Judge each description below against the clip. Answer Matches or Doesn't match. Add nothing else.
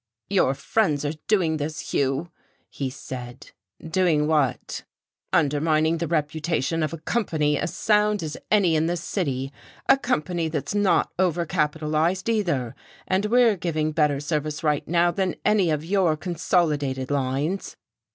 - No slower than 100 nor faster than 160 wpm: Matches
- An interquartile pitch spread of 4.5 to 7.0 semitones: Doesn't match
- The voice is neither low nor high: Matches